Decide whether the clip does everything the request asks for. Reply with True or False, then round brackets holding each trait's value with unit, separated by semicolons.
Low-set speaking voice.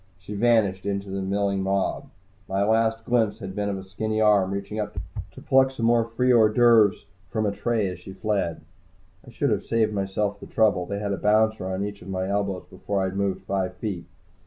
True (100 Hz)